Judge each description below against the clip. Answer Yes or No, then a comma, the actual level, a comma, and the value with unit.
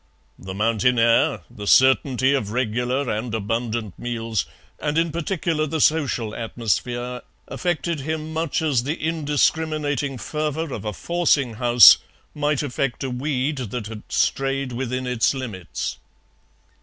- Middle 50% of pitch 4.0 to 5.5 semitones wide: Yes, average, 4.6 semitones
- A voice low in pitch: Yes, low, 130 Hz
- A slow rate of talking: Yes, slow, 130 wpm